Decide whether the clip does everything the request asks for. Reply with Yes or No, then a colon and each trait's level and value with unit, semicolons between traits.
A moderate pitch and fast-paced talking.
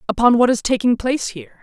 No: high, 240 Hz; fast, 220 wpm